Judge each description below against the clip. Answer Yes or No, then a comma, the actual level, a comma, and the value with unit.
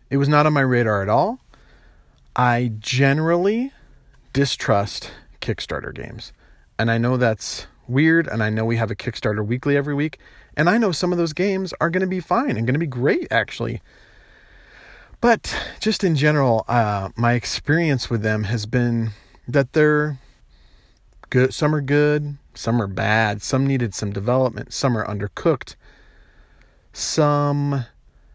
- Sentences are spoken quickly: No, average, 155 wpm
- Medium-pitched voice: No, low, 130 Hz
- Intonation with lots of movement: No, average, 4.8 semitones